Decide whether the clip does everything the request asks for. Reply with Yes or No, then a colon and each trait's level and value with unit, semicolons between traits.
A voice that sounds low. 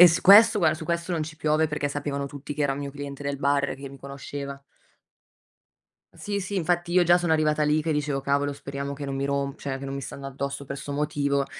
No: medium, 145 Hz